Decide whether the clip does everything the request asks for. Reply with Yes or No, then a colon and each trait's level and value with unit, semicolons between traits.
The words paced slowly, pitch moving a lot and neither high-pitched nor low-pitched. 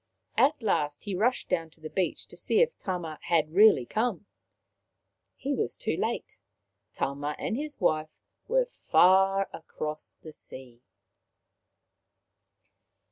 Yes: slow, 130 wpm; wide, 6.6 semitones; medium, 180 Hz